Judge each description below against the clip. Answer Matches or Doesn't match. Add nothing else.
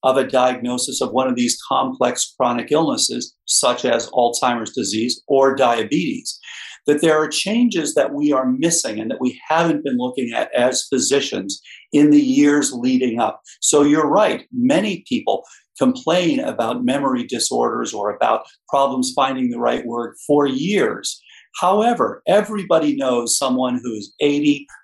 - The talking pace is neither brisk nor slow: Matches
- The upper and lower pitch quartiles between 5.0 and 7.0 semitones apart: Doesn't match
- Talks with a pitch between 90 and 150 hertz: Matches